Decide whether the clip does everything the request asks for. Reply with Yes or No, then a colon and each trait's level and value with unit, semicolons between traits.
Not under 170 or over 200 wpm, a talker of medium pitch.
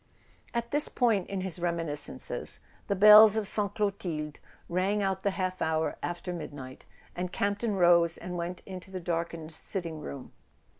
No: average, 155 wpm; medium, 180 Hz